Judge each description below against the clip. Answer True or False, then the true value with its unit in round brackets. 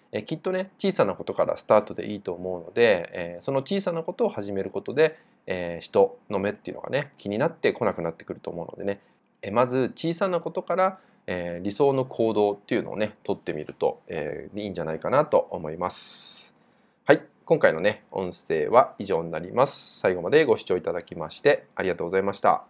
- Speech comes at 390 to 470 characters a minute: True (440 characters per minute)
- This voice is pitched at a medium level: True (165 Hz)